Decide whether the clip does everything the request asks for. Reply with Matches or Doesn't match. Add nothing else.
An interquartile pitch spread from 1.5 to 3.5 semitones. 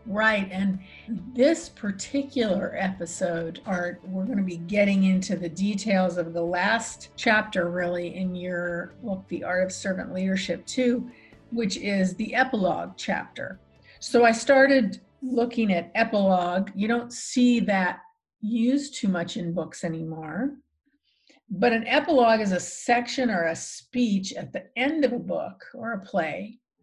Doesn't match